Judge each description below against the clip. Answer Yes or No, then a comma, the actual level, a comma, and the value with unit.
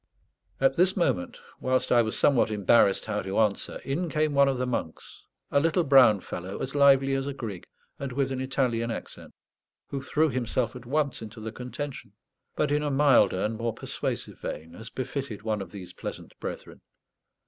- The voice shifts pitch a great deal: No, average, 4.2 semitones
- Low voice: Yes, low, 130 Hz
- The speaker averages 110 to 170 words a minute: No, average, 185 wpm